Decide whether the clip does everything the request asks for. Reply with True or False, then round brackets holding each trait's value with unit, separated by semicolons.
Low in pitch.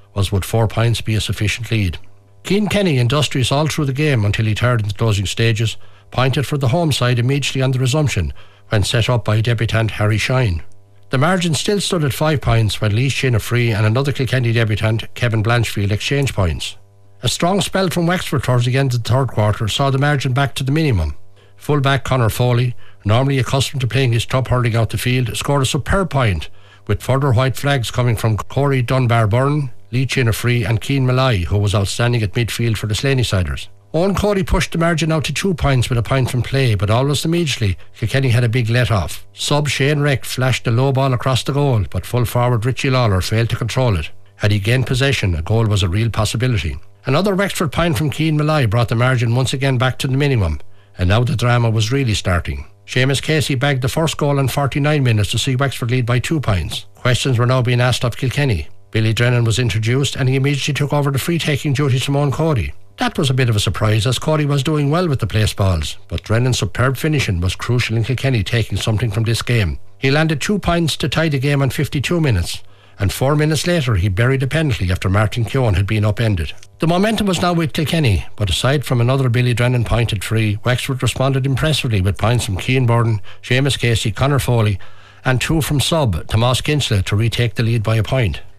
True (125 Hz)